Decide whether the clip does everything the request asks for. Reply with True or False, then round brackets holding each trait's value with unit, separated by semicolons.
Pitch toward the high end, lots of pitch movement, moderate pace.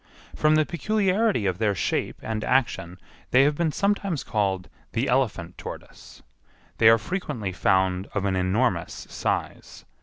False (115 Hz; 8.4 semitones; 145 wpm)